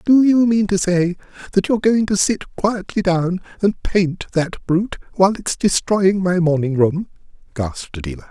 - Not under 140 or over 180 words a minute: Yes, average, 175 wpm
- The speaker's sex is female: No, male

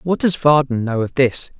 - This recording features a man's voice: Yes, male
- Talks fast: Yes, fast, 225 wpm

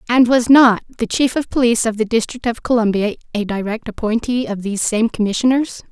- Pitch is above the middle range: Yes, high, 230 Hz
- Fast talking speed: No, average, 195 wpm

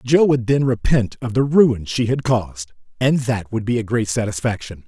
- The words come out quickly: Yes, fast, 210 wpm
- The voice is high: No, low, 115 Hz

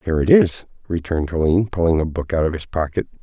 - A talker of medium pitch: No, very low, 85 Hz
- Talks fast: Yes, fast, 225 wpm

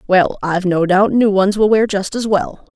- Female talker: Yes, female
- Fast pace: Yes, fast, 240 wpm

